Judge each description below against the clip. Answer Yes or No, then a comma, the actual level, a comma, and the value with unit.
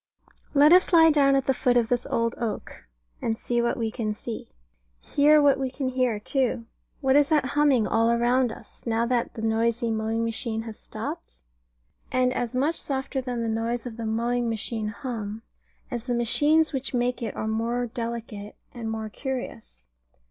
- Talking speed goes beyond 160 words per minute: Yes, average, 185 wpm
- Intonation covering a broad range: No, average, 2.9 semitones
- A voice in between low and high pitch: No, high, 240 Hz